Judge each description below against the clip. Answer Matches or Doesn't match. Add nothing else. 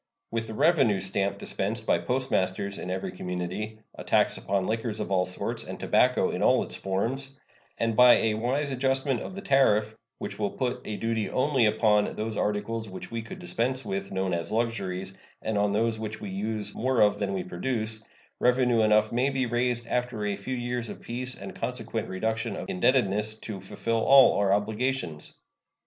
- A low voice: Matches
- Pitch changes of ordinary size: Matches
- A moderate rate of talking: Matches